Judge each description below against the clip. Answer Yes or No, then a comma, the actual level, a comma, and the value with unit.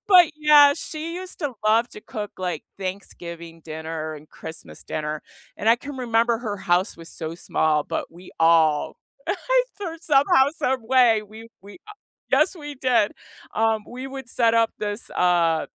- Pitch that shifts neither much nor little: No, wide, 7.8 semitones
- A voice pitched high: Yes, high, 220 Hz